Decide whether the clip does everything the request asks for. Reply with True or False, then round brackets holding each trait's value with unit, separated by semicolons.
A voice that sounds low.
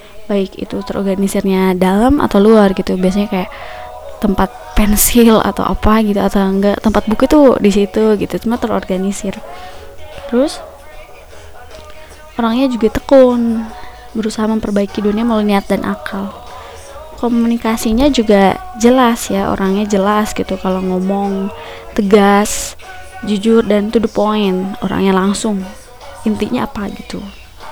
False (210 Hz)